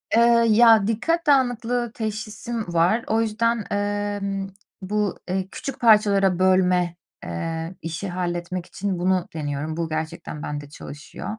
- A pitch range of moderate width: Yes, average, 4.5 semitones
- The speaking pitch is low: No, high, 195 Hz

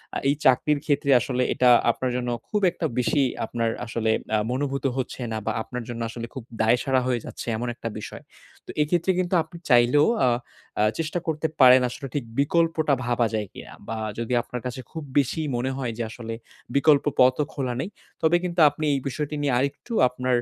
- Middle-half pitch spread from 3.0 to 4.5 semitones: Yes, average, 3.6 semitones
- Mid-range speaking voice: No, low, 130 Hz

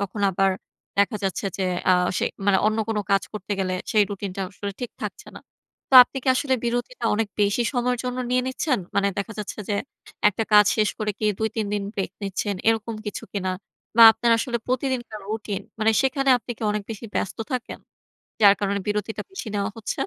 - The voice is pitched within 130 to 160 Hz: No, high, 215 Hz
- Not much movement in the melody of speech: No, average, 3.0 semitones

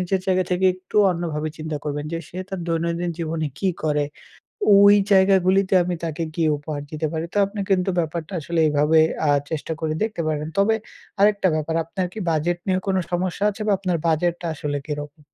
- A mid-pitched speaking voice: Yes, medium, 170 Hz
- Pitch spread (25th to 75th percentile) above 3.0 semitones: Yes, average, 3.4 semitones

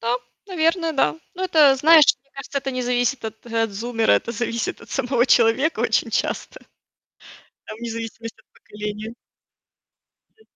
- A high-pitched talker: Yes, high, 240 Hz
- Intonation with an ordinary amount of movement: Yes, average, 3.5 semitones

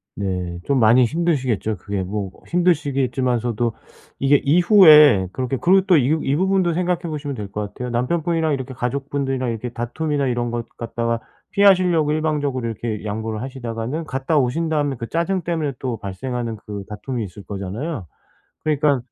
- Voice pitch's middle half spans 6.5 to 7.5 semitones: No, average, 5.3 semitones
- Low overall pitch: Yes, low, 130 Hz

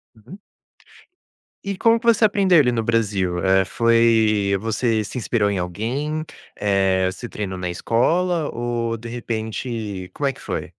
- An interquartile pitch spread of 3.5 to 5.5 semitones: Yes, average, 4.7 semitones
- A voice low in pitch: Yes, low, 115 Hz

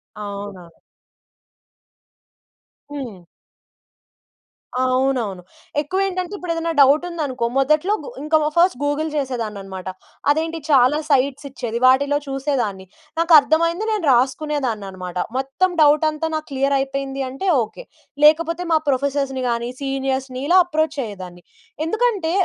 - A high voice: Yes, very high, 275 Hz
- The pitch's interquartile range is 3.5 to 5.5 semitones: Yes, average, 4.1 semitones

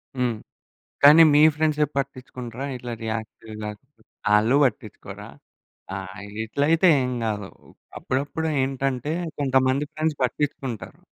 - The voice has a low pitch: Yes, low, 130 Hz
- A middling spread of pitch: Yes, average, 4.2 semitones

